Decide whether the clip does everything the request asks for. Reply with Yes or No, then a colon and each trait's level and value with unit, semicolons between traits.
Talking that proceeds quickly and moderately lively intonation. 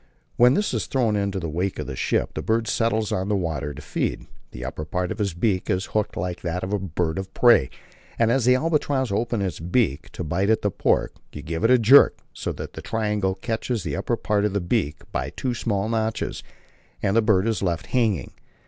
Yes: fast, 225 wpm; average, 4.4 semitones